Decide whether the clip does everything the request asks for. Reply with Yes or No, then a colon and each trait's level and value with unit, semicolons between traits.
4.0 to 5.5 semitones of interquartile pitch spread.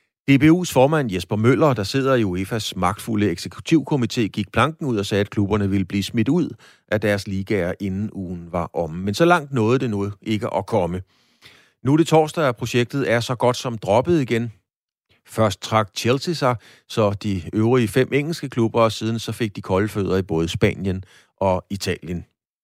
Yes: average, 4.4 semitones